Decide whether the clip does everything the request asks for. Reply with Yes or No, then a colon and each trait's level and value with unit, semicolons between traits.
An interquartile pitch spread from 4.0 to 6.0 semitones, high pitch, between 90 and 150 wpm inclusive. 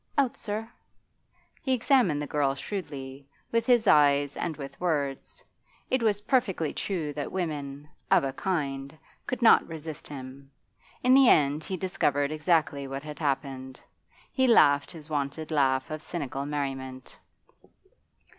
No: average, 5.1 semitones; medium, 150 Hz; average, 140 wpm